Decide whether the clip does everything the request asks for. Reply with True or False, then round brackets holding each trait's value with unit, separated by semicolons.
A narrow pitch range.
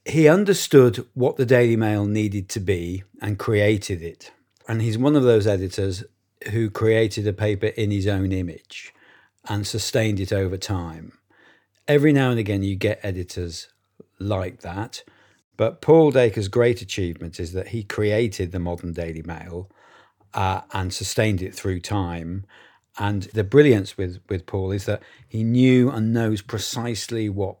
False (3.1 semitones)